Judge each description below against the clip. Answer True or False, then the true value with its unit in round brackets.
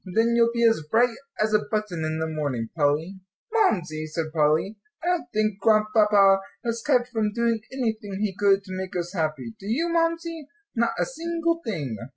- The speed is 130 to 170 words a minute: False (185 wpm)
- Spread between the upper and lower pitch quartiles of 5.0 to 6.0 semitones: True (5.6 semitones)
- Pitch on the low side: False (215 Hz)